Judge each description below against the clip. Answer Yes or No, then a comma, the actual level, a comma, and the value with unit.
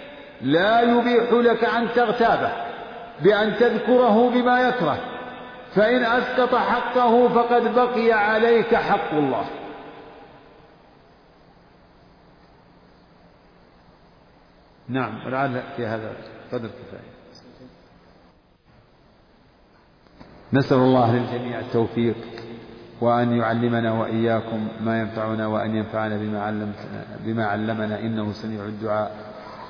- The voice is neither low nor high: No, low, 120 Hz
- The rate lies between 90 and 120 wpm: No, average, 80 wpm